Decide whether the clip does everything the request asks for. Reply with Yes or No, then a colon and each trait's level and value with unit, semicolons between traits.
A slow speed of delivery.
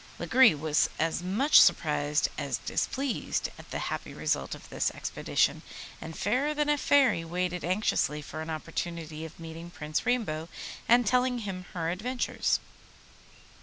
No: average, 145 wpm